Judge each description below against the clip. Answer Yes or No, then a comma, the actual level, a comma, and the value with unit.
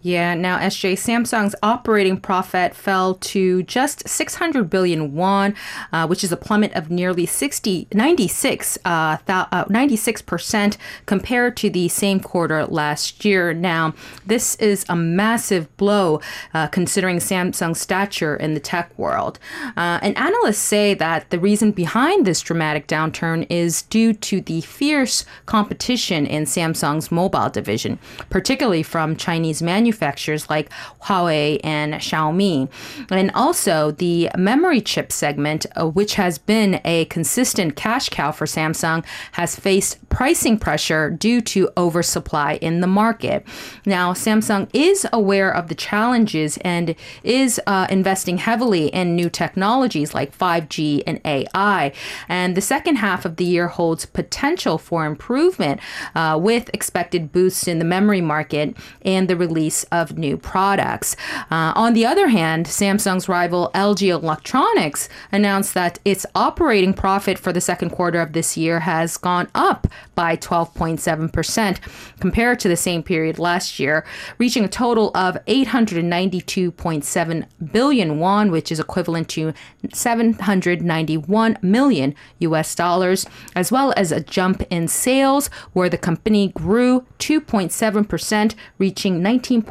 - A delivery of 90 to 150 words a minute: Yes, average, 140 wpm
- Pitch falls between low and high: Yes, medium, 180 Hz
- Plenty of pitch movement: No, average, 4.2 semitones